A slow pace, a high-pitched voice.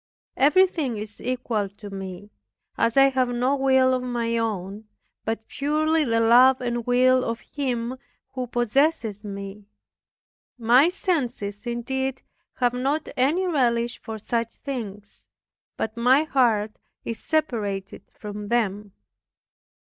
Yes: slow, 125 wpm; high, 240 Hz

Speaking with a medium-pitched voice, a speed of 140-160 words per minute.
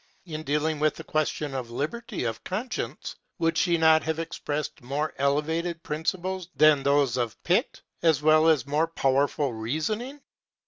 Yes: medium, 155 Hz; average, 150 wpm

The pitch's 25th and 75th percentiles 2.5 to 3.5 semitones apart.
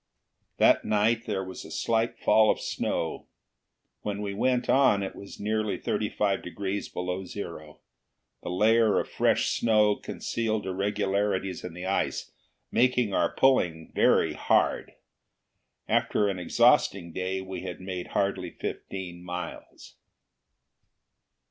Yes: average, 2.8 semitones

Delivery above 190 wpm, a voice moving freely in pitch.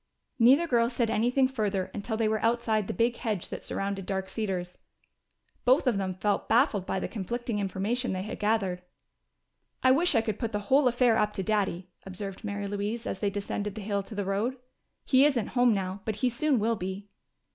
No: average, 200 wpm; average, 3.4 semitones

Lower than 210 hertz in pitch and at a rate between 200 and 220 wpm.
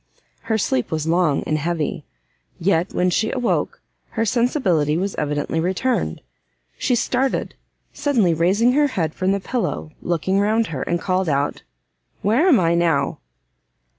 No: medium, 185 Hz; average, 145 wpm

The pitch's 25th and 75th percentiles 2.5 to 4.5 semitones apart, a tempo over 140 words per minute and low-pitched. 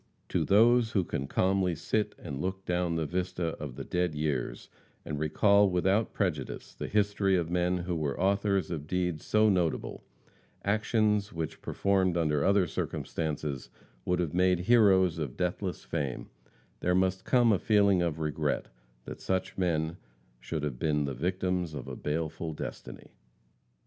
Yes: average, 3.8 semitones; average, 155 wpm; very low, 90 Hz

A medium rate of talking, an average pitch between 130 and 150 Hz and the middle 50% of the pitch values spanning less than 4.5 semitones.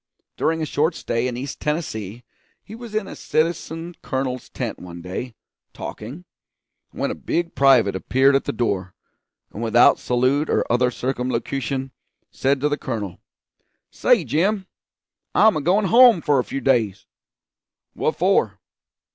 No: average, 145 wpm; low, 135 Hz; average, 5.3 semitones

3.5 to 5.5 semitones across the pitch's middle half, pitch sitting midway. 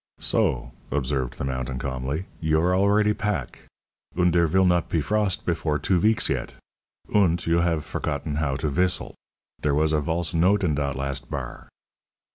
No: average, 4.3 semitones; very low, 80 Hz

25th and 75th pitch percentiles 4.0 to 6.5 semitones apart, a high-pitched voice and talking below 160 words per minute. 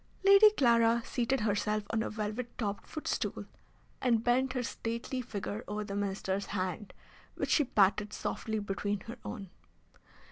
No: average, 3.0 semitones; high, 220 Hz; average, 145 wpm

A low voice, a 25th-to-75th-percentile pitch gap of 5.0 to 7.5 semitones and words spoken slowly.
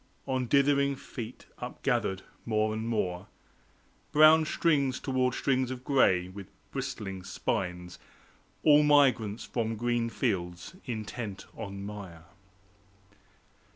Yes: low, 115 Hz; average, 5.3 semitones; slow, 105 wpm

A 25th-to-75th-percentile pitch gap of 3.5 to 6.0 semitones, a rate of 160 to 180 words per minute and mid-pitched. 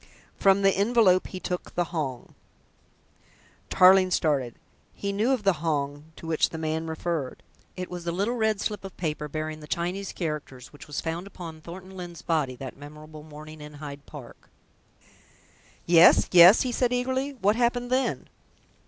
Yes: average, 4.5 semitones; average, 165 wpm; medium, 170 Hz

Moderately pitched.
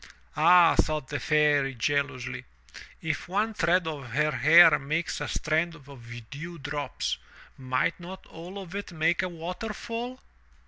Yes: medium, 160 Hz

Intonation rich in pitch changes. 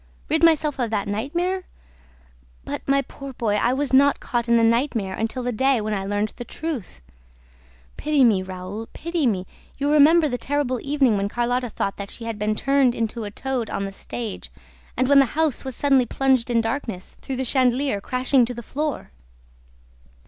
No: average, 4.2 semitones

